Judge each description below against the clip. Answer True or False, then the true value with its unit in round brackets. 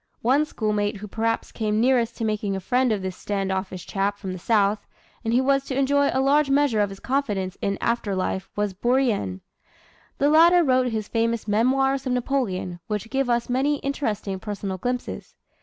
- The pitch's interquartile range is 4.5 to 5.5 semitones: True (4.8 semitones)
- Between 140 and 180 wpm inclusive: False (190 wpm)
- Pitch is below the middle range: False (225 Hz)